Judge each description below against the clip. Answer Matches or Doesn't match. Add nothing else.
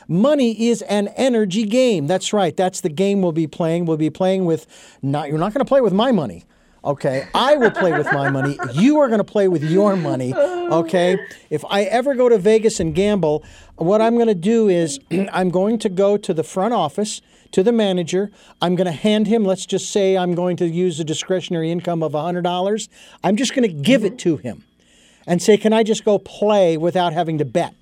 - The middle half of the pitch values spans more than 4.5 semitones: Doesn't match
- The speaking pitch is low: Doesn't match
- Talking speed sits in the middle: Doesn't match